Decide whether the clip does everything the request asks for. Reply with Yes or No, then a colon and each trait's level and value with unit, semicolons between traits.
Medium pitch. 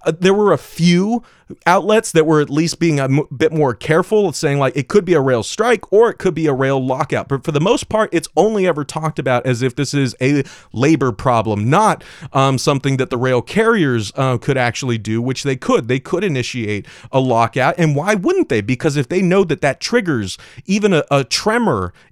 Yes: medium, 145 Hz